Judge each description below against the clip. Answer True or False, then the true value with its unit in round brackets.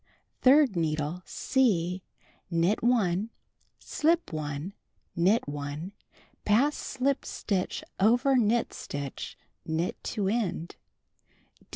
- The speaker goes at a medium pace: False (95 wpm)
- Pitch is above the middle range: True (195 Hz)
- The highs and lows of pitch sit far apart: True (6.4 semitones)